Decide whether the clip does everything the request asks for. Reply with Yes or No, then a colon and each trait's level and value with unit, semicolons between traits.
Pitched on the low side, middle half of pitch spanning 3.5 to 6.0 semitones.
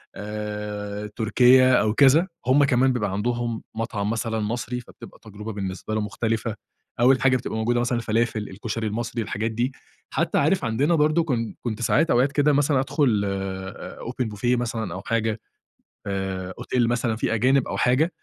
No: low, 115 Hz; average, 3.1 semitones